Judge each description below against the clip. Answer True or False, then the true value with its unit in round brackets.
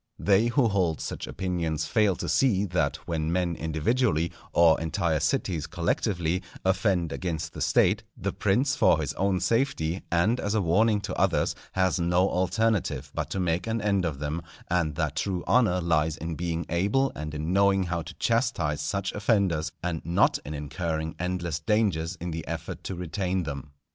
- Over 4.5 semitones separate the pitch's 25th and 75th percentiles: False (3.6 semitones)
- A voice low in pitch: True (90 Hz)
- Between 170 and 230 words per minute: True (175 wpm)